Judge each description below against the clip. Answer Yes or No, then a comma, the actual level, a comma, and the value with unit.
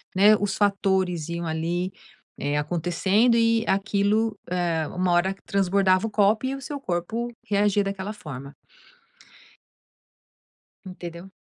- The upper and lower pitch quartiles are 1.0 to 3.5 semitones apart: Yes, average, 3.2 semitones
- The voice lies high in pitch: Yes, high, 195 Hz